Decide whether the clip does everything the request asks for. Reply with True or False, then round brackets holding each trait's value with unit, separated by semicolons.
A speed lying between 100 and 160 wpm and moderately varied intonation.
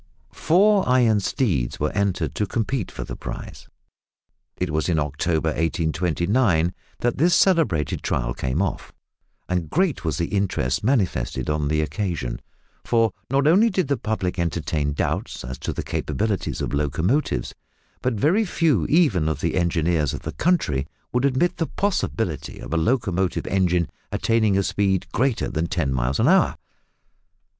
False (155 wpm; 8.4 semitones)